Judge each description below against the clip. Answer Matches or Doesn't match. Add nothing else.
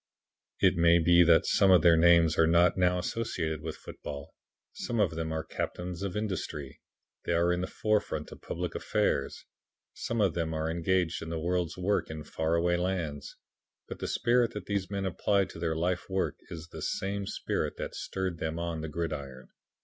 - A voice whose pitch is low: Matches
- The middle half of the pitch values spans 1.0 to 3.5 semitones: Matches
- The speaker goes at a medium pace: Matches